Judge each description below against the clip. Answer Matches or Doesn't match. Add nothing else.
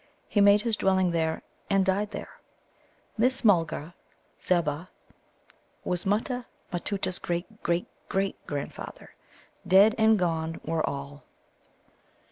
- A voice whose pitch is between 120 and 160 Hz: Doesn't match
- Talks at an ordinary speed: Doesn't match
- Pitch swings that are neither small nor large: Matches